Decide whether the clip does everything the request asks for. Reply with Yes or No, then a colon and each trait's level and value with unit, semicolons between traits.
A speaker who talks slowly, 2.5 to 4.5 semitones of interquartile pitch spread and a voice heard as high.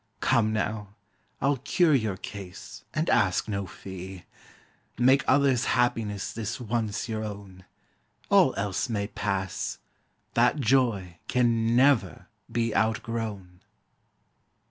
No: slow, 110 wpm; average, 3.5 semitones; low, 110 Hz